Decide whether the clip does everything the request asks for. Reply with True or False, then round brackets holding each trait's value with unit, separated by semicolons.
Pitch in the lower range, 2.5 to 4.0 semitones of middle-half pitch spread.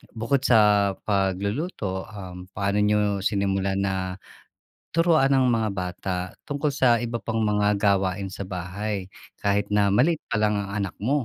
True (105 Hz; 2.8 semitones)